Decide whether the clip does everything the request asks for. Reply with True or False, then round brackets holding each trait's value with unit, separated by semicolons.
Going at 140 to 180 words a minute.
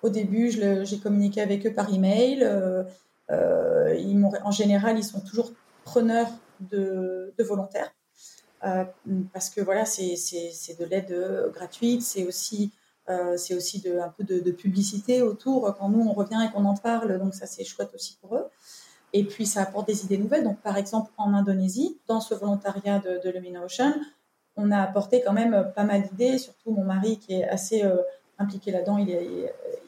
False (195 wpm)